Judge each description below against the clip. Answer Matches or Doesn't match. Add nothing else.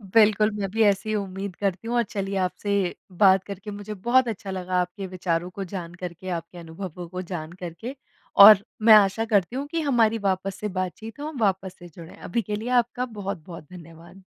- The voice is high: Matches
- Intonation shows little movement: Doesn't match